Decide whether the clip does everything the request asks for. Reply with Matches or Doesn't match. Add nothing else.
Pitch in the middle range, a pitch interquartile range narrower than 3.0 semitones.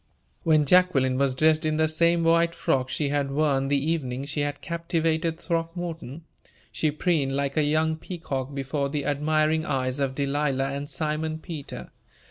Matches